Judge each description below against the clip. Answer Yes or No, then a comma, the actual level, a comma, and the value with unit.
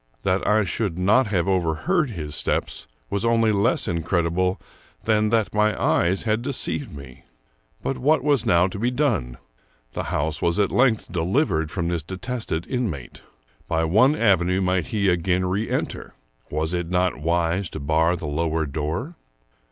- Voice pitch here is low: Yes, very low, 95 Hz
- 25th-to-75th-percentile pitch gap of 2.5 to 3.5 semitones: No, average, 5.1 semitones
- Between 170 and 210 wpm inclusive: No, average, 160 wpm